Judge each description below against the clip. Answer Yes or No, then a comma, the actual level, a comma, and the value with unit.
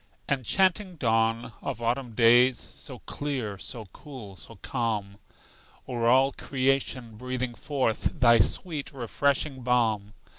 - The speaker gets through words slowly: Yes, slow, 115 wpm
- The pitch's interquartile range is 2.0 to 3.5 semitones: Yes, average, 3.0 semitones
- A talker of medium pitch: No, low, 125 Hz